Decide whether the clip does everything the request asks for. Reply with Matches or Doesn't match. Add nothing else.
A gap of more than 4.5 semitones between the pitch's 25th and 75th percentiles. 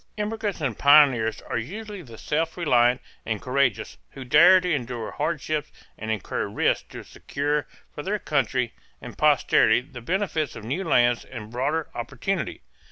Matches